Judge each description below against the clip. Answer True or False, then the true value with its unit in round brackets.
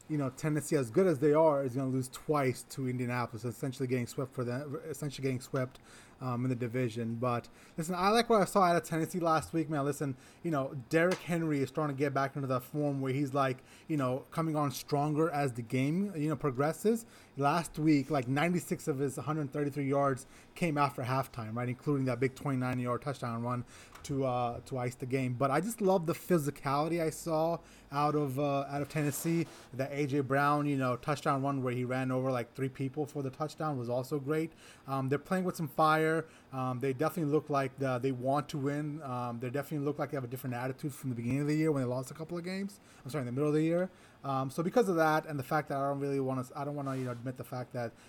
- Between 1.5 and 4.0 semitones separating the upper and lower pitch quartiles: True (3.1 semitones)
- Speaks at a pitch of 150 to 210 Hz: False (140 Hz)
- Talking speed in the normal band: False (245 wpm)